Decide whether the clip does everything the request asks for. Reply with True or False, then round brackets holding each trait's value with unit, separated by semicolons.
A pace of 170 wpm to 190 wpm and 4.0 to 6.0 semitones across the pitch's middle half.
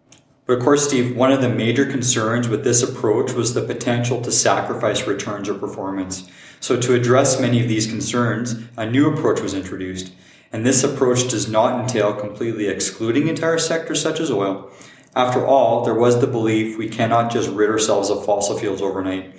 False (185 wpm; 3.6 semitones)